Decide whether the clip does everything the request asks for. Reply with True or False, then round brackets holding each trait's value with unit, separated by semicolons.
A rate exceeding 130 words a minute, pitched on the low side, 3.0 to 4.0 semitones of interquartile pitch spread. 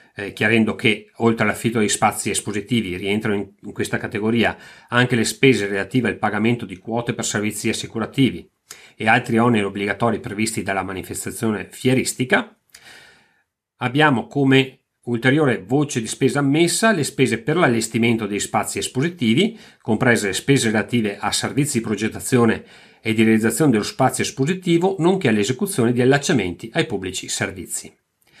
True (140 wpm; 115 Hz; 3.6 semitones)